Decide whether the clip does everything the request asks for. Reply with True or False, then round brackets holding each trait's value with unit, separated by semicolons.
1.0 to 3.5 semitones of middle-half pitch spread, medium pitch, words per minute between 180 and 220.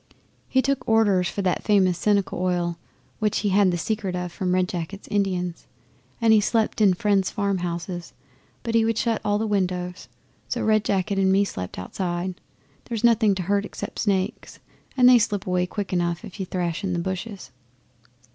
False (2.8 semitones; 195 Hz; 185 wpm)